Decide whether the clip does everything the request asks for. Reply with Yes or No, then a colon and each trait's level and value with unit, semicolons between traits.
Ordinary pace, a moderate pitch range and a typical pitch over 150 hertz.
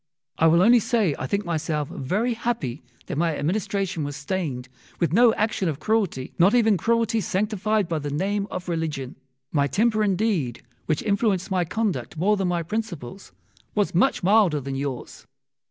No: average, 170 wpm; wide, 5.9 semitones; medium, 185 Hz